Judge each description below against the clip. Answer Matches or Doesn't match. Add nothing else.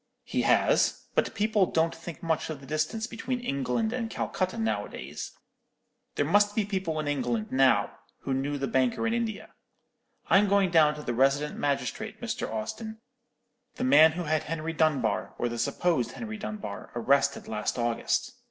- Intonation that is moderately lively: Doesn't match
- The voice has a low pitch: Doesn't match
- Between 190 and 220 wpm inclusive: Doesn't match